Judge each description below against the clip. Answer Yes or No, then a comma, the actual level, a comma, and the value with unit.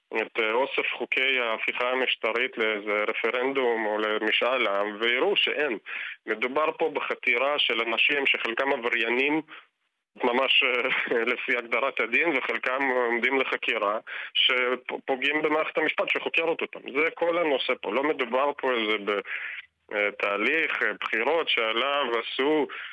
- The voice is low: Yes, low, 125 Hz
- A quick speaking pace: No, average, 115 wpm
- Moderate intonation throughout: No, wide, 5.7 semitones